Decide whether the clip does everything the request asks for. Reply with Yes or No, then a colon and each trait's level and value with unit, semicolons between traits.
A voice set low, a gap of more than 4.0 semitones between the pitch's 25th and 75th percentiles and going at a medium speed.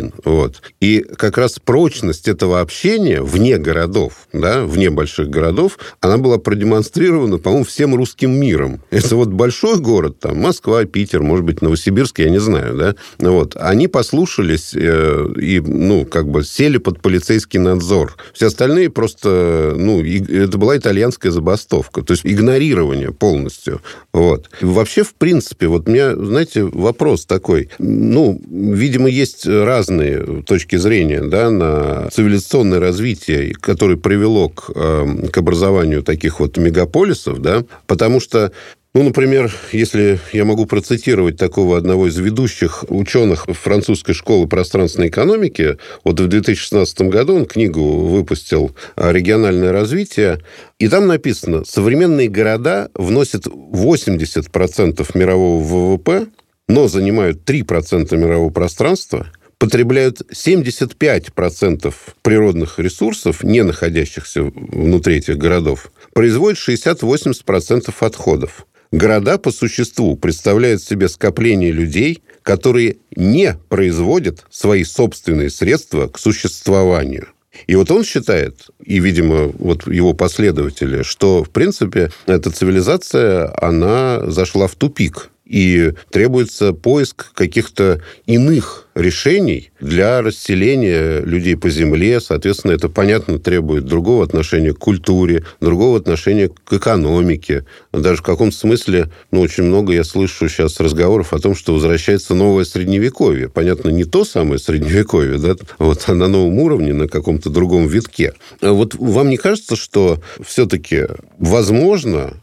Yes: very low, 95 Hz; average, 4.7 semitones; average, 125 wpm